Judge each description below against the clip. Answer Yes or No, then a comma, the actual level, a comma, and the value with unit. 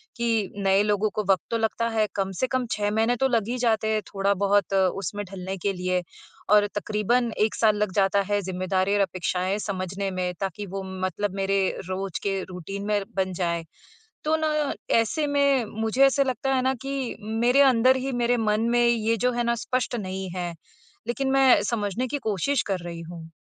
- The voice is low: No, high, 210 Hz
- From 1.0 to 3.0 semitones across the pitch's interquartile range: No, average, 3.8 semitones